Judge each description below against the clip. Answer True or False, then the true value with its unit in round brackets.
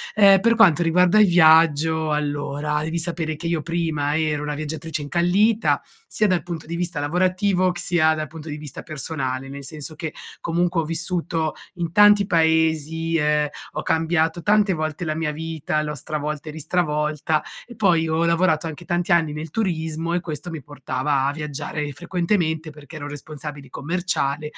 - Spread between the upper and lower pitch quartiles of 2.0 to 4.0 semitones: True (2.4 semitones)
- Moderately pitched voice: True (160 Hz)